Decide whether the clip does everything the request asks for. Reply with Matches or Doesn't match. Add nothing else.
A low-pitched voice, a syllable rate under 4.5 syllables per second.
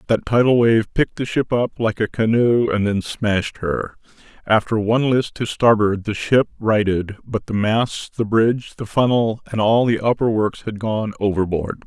Doesn't match